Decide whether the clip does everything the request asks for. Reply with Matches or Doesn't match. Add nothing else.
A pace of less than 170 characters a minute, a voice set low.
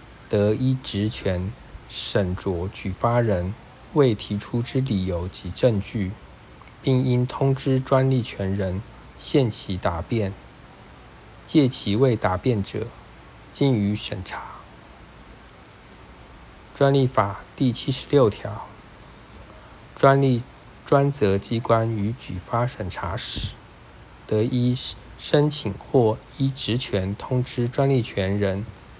Matches